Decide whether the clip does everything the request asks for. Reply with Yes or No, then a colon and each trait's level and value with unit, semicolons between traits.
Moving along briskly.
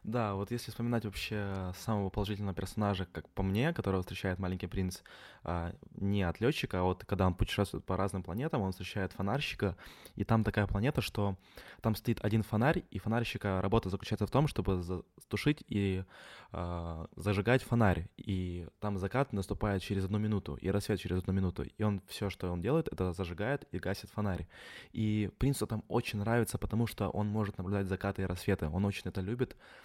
Yes: fast, 180 wpm